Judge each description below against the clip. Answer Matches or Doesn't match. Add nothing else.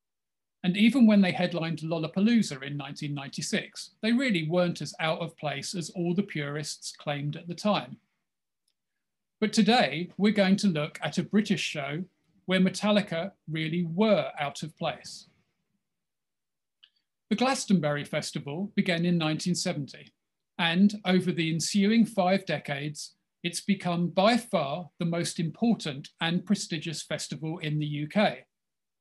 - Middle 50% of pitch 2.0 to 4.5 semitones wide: Matches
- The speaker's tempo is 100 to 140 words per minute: Matches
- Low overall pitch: Doesn't match